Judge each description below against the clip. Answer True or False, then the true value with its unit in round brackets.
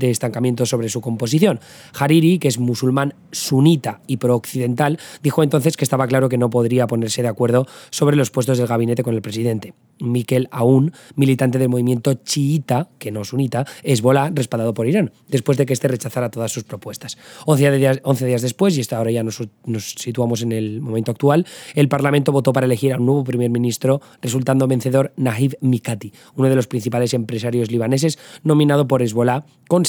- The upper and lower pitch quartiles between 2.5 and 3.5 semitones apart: True (2.8 semitones)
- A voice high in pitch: False (130 Hz)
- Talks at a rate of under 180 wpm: False (185 wpm)